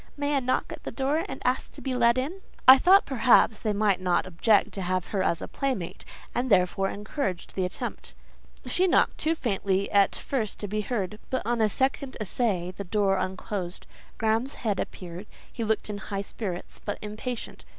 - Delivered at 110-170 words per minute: No, average, 190 wpm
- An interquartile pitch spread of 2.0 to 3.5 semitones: No, average, 4.9 semitones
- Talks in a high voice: Yes, high, 215 Hz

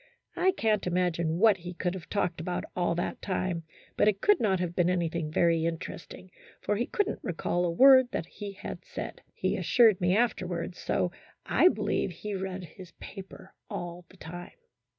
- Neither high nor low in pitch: Yes, medium, 180 Hz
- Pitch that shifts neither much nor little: Yes, average, 3.0 semitones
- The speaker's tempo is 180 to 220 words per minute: Yes, average, 185 wpm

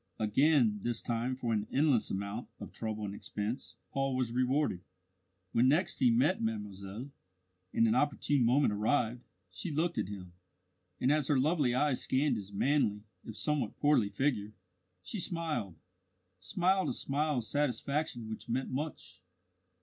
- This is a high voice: No, low, 125 Hz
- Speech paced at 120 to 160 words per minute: Yes, average, 150 wpm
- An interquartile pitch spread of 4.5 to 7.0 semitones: Yes, average, 5.2 semitones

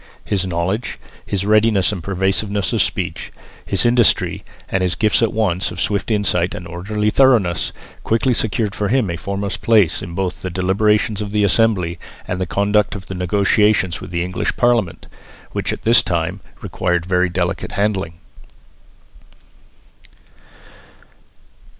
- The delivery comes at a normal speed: Yes, average, 150 wpm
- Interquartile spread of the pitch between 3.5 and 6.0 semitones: No, average, 2.9 semitones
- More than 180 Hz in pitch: No, low, 100 Hz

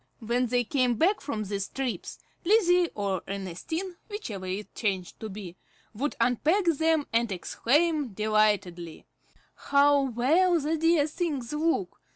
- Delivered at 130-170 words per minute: Yes, slow, 135 wpm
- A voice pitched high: Yes, very high, 250 Hz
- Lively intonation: Yes, wide, 7.7 semitones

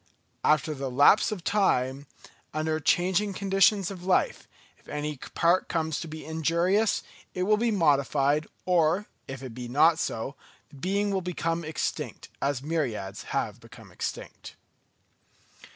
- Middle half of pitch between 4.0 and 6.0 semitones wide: Yes, average, 4.6 semitones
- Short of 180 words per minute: Yes, average, 140 wpm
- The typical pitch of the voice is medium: Yes, medium, 160 Hz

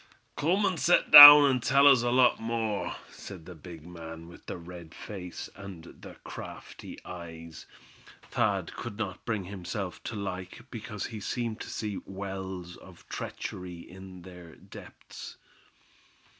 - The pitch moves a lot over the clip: No, average, 4.7 semitones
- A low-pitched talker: Yes, very low, 95 Hz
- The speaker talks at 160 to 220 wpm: No, average, 145 wpm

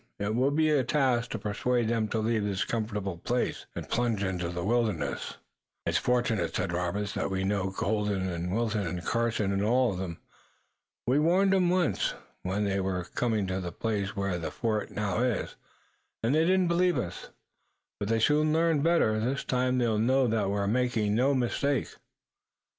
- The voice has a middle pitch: No, low, 110 Hz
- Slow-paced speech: No, average, 180 wpm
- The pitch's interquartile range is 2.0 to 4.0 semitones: No, average, 4.4 semitones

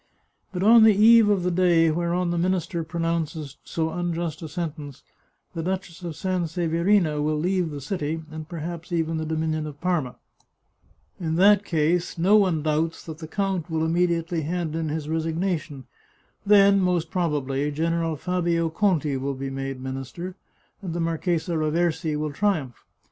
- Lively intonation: No, narrow, 2.5 semitones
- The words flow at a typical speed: Yes, average, 160 wpm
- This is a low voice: No, medium, 165 Hz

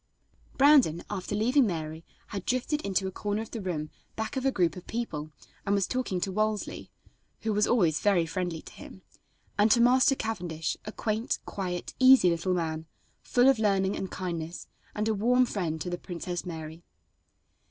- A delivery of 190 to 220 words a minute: No, average, 180 wpm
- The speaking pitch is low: No, high, 195 Hz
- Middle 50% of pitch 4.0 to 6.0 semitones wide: Yes, average, 4.5 semitones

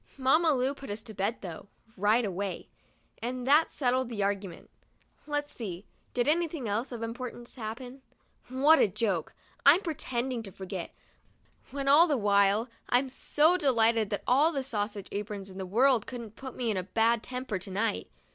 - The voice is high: Yes, high, 235 Hz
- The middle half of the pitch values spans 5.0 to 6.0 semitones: No, average, 4.6 semitones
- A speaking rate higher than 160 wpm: Yes, average, 175 wpm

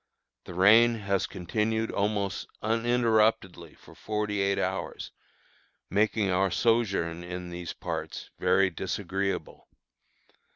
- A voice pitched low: Yes, low, 100 Hz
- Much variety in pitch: No, average, 3.2 semitones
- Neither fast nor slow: No, slow, 100 wpm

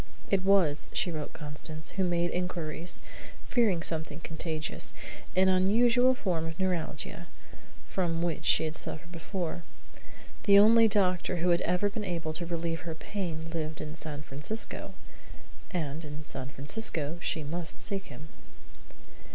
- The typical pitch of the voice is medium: Yes, medium, 170 Hz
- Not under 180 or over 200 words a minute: No, average, 145 wpm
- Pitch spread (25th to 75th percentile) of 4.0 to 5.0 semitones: No, average, 3.2 semitones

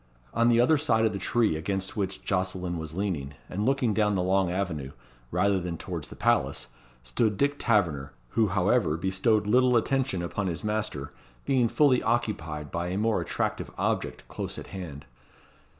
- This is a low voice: Yes, low, 100 Hz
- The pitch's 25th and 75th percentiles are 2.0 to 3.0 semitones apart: No, average, 4.7 semitones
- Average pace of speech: Yes, average, 170 wpm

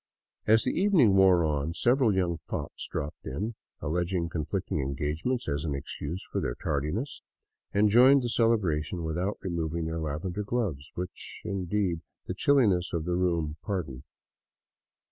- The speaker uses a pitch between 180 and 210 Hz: No, very low, 90 Hz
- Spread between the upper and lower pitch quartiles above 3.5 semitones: Yes, average, 5.1 semitones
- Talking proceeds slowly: No, average, 145 wpm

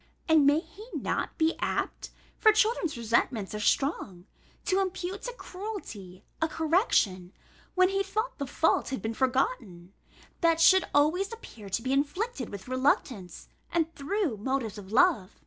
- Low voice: No, very high, 290 Hz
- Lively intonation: Yes, wide, 9.0 semitones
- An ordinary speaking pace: Yes, average, 150 wpm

